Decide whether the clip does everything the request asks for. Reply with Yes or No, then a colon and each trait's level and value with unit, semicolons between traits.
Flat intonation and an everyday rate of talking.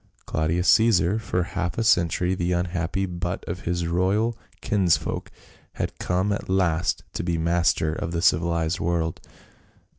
Yes: narrow, 1.8 semitones; average, 145 wpm